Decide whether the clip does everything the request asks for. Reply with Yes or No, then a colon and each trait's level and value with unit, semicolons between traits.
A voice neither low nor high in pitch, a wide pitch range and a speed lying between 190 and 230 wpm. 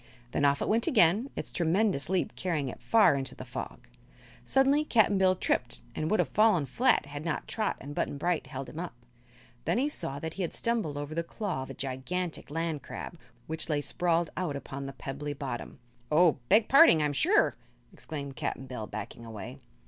Yes: medium, 160 Hz; wide, 5.8 semitones; average, 195 wpm